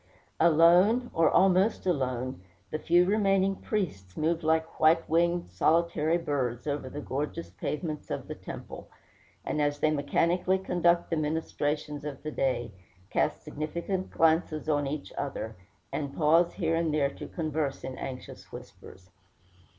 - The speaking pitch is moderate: Yes, medium, 155 Hz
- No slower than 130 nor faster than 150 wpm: Yes, average, 145 wpm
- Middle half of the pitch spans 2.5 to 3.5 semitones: Yes, average, 3.0 semitones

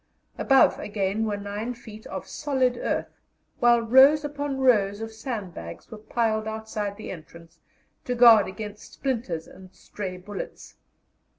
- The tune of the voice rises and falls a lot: No, average, 3.5 semitones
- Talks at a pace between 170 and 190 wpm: No, slow, 135 wpm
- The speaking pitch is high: Yes, high, 220 Hz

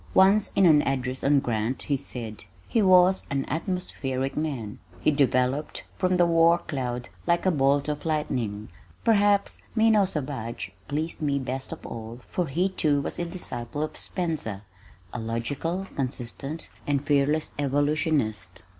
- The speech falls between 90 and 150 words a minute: Yes, average, 145 wpm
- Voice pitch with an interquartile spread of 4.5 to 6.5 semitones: Yes, average, 4.8 semitones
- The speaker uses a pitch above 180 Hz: No, medium, 145 Hz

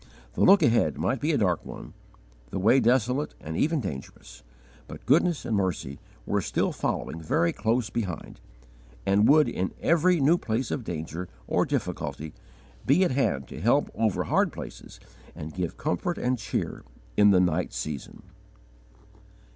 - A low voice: Yes, low, 110 Hz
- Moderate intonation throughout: No, wide, 8.0 semitones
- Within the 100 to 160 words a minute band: Yes, average, 155 wpm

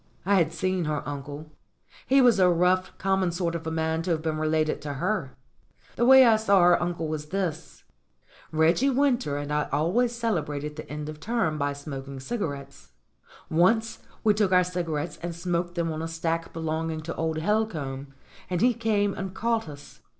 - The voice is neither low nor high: Yes, medium, 165 Hz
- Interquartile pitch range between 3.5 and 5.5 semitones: Yes, average, 4.0 semitones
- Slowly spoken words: No, average, 185 wpm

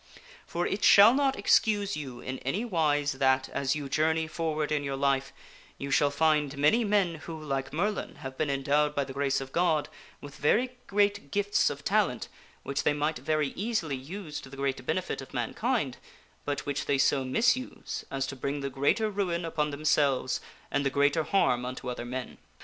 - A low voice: No, medium, 150 Hz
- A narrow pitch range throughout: No, average, 3.9 semitones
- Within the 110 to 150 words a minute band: No, average, 190 wpm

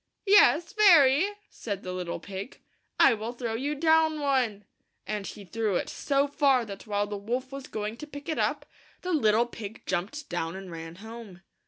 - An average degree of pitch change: No, wide, 6.1 semitones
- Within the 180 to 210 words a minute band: Yes, average, 190 wpm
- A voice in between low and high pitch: No, high, 230 Hz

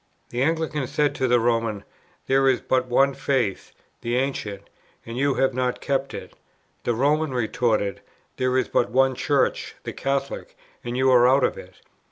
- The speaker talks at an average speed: Yes, average, 180 wpm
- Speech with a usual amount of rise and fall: No, narrow, 2.2 semitones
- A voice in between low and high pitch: No, low, 130 Hz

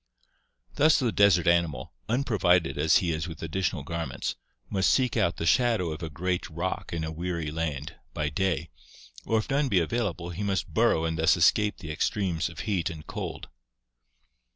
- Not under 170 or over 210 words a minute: Yes, average, 180 wpm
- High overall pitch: No, very low, 85 Hz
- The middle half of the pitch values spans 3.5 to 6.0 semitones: Yes, average, 3.8 semitones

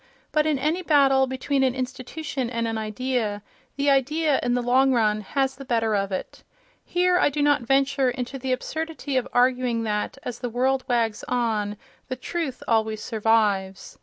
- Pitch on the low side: No, very high, 255 Hz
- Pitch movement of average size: Yes, average, 3.3 semitones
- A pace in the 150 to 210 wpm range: Yes, average, 175 wpm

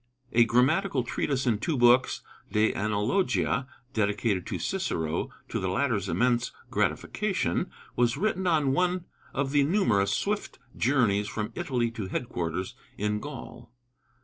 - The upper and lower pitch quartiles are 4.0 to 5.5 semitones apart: Yes, average, 5.2 semitones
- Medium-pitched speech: No, low, 120 Hz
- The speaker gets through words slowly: Yes, slow, 130 wpm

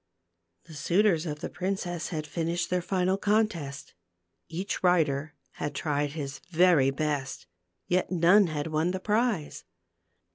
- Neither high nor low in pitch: Yes, medium, 165 Hz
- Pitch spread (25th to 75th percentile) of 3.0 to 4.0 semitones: Yes, average, 3.7 semitones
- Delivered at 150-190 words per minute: No, slow, 135 wpm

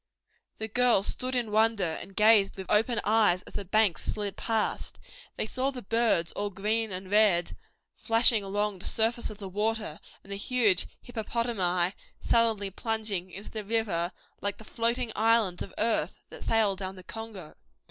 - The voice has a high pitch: Yes, high, 215 Hz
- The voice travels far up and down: No, average, 2.7 semitones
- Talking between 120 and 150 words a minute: No, average, 170 wpm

